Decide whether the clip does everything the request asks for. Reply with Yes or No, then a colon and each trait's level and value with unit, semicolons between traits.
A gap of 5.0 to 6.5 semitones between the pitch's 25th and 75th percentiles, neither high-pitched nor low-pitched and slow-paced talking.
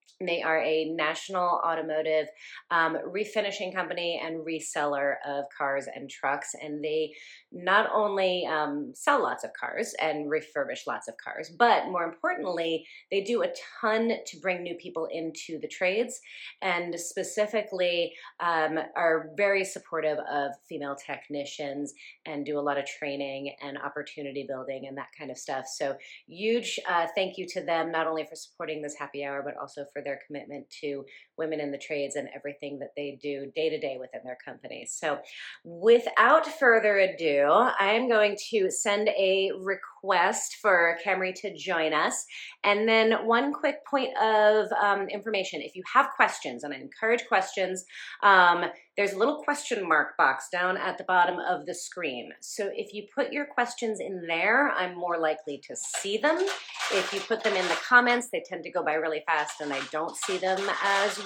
No: wide, 5.5 semitones; medium, 170 Hz; average, 175 wpm